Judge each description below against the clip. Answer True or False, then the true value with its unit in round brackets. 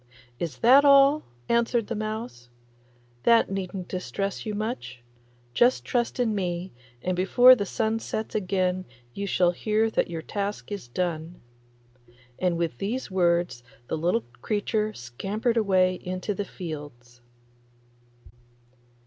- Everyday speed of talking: False (130 wpm)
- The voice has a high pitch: True (195 Hz)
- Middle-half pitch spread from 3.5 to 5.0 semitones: True (4.1 semitones)